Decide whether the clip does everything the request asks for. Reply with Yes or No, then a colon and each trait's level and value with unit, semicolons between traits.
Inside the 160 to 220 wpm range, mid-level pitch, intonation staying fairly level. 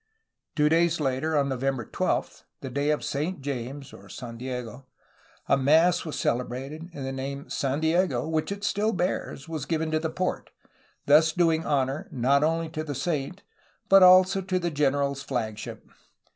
No: average, 170 wpm; medium, 150 Hz; average, 3.5 semitones